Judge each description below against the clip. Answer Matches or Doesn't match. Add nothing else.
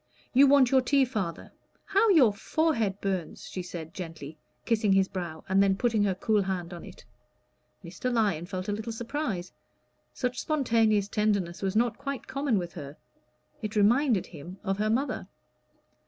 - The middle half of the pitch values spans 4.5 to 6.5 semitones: Matches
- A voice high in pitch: Matches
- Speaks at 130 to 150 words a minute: Doesn't match